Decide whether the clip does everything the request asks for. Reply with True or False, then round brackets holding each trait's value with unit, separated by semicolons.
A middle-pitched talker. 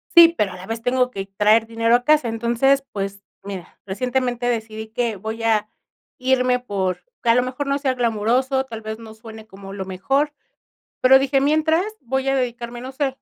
False (240 Hz)